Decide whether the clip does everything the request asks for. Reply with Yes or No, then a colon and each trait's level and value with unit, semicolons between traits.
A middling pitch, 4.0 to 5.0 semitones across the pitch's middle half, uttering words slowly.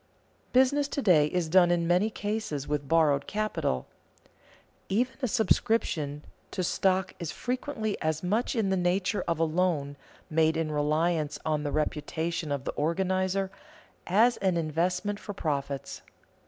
No: medium, 175 Hz; average, 4.7 semitones; average, 150 wpm